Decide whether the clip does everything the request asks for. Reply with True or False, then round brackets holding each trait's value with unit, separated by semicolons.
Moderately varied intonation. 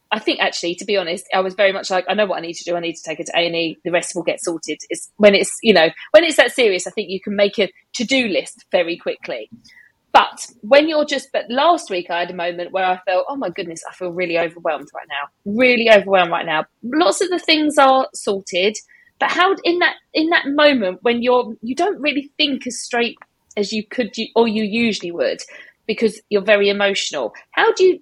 False (7.2 semitones)